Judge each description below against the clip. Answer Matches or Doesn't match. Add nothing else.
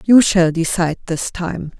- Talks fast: Doesn't match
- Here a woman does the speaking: Matches